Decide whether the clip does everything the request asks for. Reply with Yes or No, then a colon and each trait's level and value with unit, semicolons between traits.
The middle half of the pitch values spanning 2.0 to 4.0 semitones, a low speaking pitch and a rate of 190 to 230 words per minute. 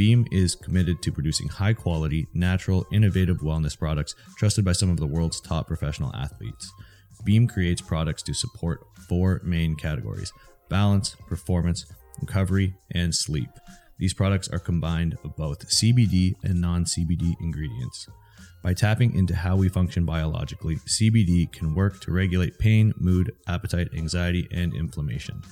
No: average, 2.8 semitones; very low, 90 Hz; average, 145 wpm